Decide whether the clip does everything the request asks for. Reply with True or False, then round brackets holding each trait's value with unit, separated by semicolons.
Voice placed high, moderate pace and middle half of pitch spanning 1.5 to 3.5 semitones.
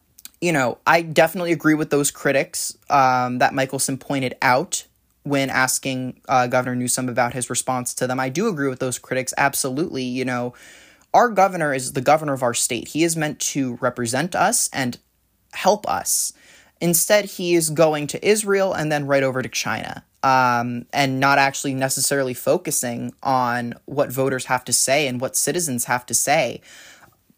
False (135 Hz; 175 wpm; 2.9 semitones)